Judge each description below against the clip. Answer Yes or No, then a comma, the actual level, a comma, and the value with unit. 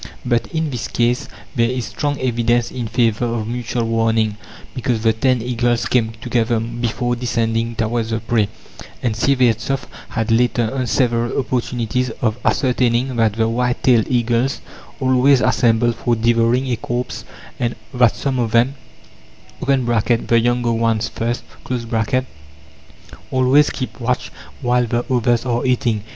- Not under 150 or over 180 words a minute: No, average, 140 wpm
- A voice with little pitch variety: Yes, narrow, 1.6 semitones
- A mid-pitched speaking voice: No, low, 120 Hz